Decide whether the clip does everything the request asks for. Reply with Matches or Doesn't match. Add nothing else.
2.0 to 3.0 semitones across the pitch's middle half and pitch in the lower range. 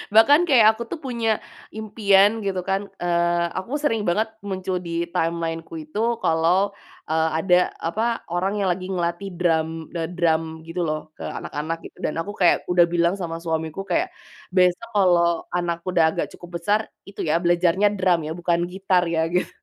Doesn't match